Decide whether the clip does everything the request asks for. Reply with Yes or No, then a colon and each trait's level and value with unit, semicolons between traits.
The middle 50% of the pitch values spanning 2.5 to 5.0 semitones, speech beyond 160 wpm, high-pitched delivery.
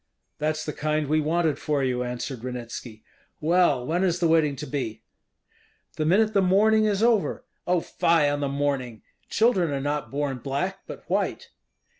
No: average, 4.6 semitones; average, 170 wpm; medium, 150 Hz